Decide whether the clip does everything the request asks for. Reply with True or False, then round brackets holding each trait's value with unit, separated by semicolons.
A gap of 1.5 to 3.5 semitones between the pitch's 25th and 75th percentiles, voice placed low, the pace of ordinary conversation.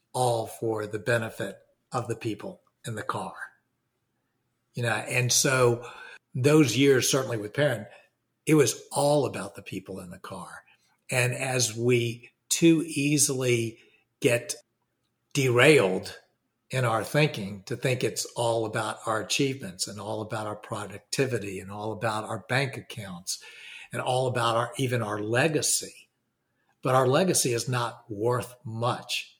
True (2.8 semitones; 120 Hz; 145 wpm)